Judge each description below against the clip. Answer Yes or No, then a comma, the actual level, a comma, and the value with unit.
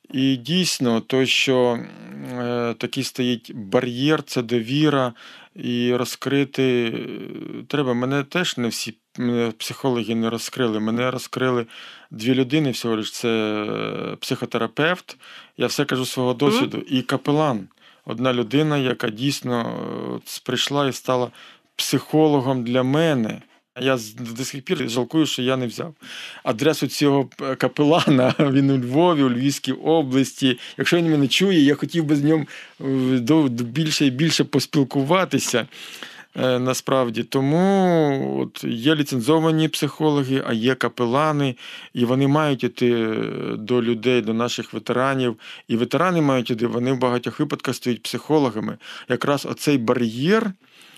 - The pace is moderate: Yes, average, 125 wpm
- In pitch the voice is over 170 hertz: No, low, 130 Hz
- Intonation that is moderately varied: Yes, average, 3.0 semitones